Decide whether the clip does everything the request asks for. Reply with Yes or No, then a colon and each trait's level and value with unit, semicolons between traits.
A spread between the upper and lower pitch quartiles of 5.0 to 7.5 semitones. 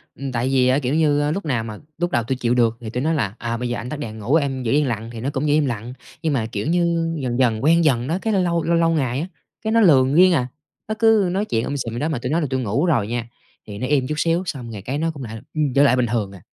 Yes: average, 5.3 semitones